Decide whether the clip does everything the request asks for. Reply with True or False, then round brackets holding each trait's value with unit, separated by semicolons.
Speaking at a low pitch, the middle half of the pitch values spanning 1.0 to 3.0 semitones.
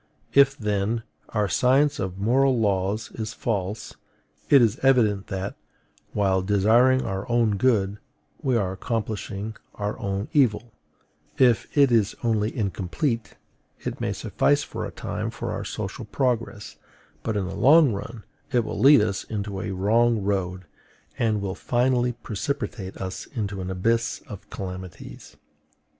False (110 Hz; 3.6 semitones)